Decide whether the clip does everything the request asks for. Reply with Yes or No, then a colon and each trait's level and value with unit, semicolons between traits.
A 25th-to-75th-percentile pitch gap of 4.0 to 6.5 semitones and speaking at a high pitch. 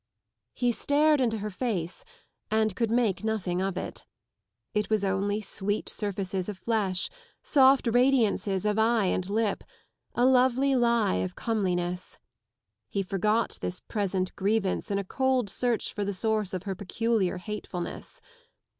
No: average, 3.4 semitones; high, 210 Hz